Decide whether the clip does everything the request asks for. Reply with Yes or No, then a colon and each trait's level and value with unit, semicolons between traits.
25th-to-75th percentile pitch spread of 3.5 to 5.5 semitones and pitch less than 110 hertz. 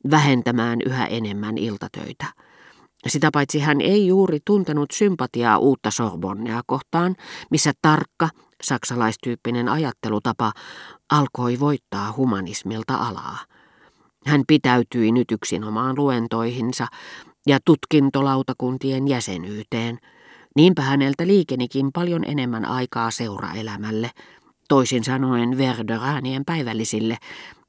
No: average, 4.1 semitones; low, 125 Hz